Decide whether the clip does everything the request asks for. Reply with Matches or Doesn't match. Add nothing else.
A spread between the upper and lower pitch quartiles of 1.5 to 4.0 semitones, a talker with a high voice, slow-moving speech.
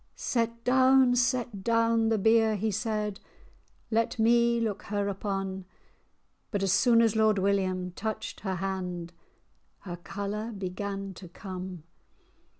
Matches